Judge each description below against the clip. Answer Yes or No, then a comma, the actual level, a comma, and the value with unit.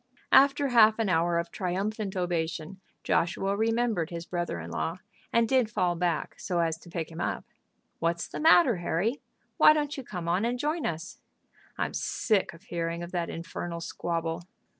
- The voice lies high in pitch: No, medium, 180 Hz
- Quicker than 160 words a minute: Yes, average, 175 wpm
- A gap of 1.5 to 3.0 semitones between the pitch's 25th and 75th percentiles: No, average, 5.0 semitones